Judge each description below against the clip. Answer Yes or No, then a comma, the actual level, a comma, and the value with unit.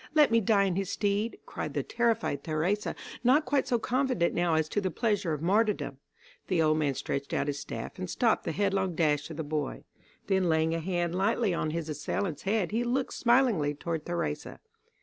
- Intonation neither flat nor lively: No, wide, 5.7 semitones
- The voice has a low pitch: No, medium, 180 Hz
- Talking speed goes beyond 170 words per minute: Yes, average, 200 wpm